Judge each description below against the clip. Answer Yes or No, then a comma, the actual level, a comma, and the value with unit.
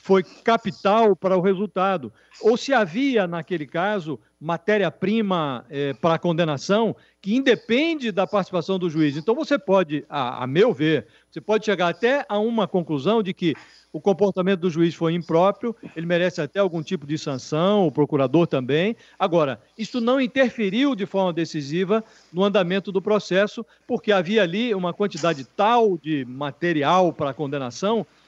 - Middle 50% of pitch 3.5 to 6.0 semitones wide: Yes, average, 4.6 semitones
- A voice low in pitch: No, high, 190 Hz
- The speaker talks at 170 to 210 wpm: No, average, 160 wpm